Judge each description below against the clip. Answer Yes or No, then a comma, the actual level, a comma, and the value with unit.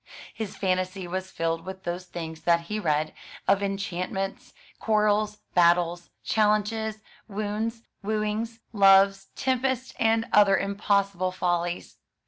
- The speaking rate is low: Yes, slow, 110 wpm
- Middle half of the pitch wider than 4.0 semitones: No, average, 3.0 semitones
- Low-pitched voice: No, high, 195 Hz